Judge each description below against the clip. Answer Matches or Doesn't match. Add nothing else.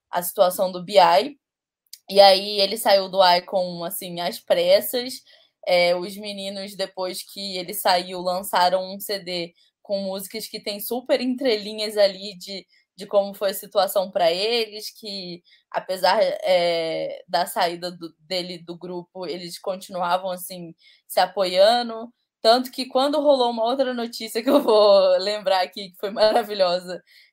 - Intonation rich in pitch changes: Doesn't match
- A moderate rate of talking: Matches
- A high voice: Matches